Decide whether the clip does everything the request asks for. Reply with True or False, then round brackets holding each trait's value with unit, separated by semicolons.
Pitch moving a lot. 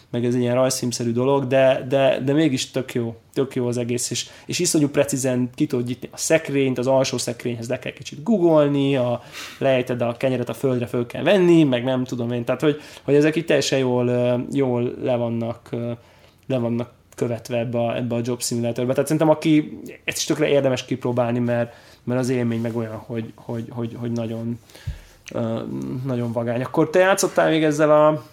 False (2.8 semitones)